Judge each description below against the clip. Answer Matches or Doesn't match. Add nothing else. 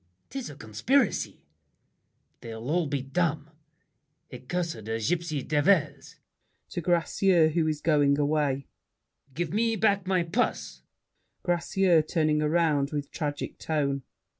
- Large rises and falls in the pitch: Doesn't match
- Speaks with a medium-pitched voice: Matches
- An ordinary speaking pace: Doesn't match